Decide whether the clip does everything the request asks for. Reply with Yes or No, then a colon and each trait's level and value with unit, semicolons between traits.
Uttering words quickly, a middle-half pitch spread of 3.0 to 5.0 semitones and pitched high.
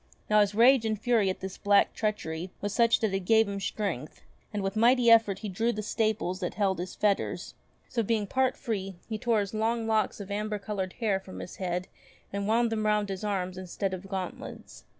No: fast, 210 wpm; narrow, 2.5 semitones; high, 205 Hz